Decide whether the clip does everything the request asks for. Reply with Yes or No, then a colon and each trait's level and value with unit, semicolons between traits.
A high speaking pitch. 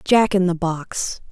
No: medium, 180 Hz